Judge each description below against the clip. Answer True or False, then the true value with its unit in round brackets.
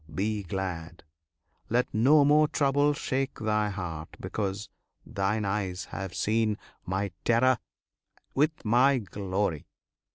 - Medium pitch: False (105 Hz)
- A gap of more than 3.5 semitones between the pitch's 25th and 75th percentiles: True (5.1 semitones)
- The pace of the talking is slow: True (110 wpm)